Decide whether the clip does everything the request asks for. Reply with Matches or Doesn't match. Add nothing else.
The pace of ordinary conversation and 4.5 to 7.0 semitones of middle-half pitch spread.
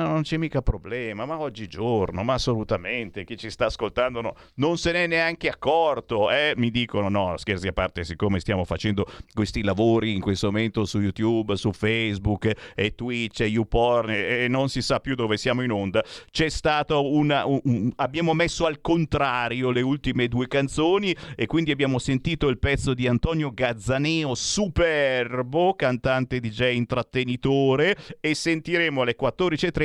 Matches